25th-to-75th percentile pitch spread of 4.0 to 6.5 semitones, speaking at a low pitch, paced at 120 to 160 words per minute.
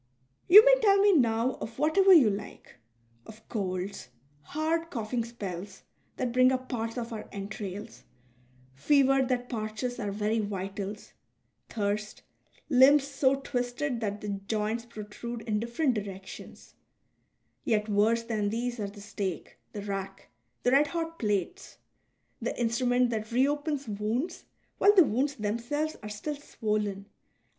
No: average, 4.5 semitones; high, 230 Hz; average, 140 wpm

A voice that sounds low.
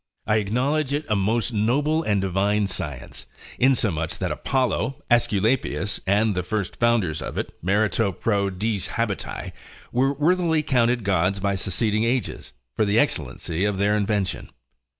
Yes: low, 105 Hz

